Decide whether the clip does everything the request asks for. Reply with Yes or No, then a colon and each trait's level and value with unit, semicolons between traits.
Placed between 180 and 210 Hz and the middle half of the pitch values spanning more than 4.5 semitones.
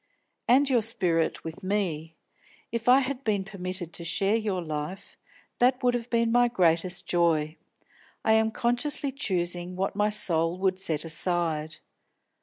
Yes: high, 190 Hz; wide, 5.5 semitones